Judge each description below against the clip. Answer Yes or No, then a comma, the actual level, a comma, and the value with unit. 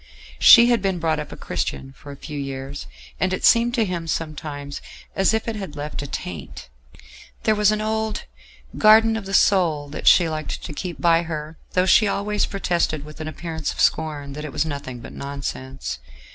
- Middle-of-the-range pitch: Yes, medium, 160 Hz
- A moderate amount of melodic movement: No, wide, 5.7 semitones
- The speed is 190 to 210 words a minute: Yes, average, 200 wpm